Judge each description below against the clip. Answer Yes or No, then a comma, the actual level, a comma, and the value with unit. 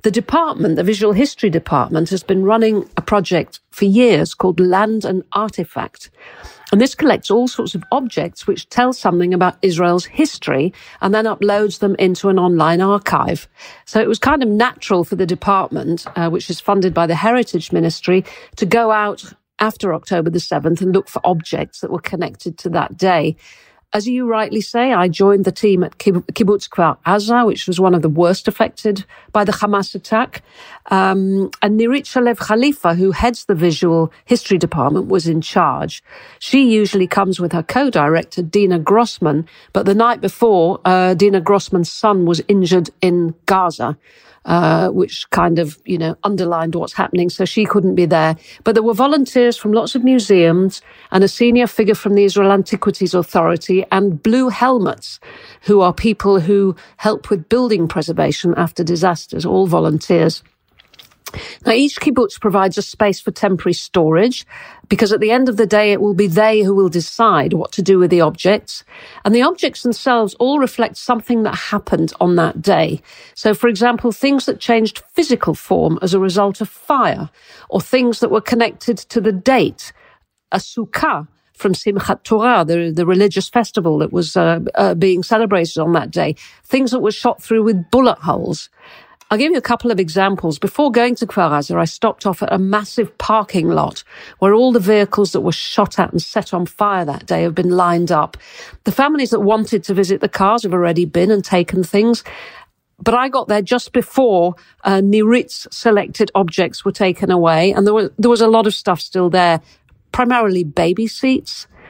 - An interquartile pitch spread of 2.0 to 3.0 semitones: No, average, 4.1 semitones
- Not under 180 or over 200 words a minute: Yes, average, 185 wpm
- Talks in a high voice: Yes, high, 200 Hz